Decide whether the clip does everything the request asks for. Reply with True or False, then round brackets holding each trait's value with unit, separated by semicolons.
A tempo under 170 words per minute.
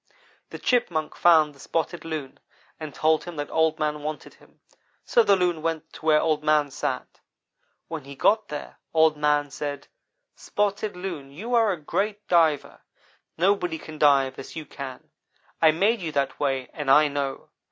False (175 wpm)